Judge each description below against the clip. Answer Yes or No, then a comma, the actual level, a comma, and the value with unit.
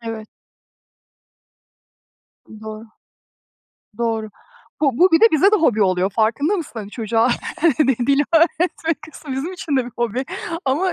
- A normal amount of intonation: No, wide, 6.4 semitones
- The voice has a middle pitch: No, very high, 260 Hz